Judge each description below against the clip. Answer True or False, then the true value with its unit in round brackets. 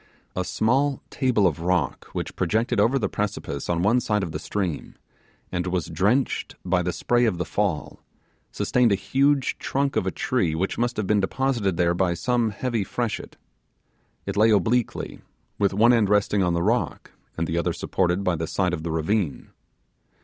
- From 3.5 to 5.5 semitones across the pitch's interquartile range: True (5.1 semitones)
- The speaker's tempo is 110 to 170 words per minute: False (185 wpm)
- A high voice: False (100 Hz)